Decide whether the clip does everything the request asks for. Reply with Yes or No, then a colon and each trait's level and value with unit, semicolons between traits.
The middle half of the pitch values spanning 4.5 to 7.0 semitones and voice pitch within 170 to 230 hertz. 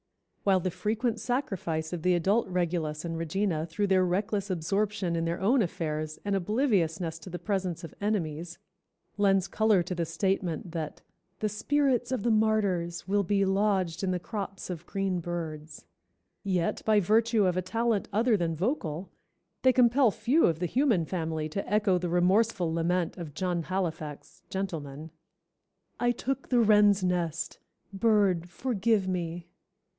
No: average, 3.9 semitones; medium, 185 Hz